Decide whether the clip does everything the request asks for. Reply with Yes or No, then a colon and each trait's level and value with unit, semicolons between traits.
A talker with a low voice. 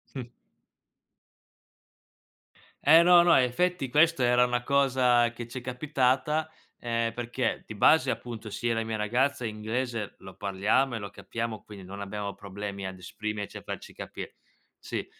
Yes: low, 120 Hz